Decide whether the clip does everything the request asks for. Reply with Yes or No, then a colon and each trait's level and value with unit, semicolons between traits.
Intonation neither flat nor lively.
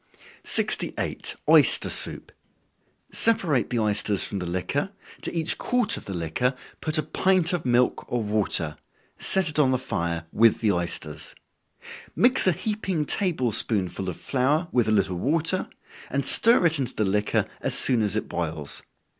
No: wide, 8.6 semitones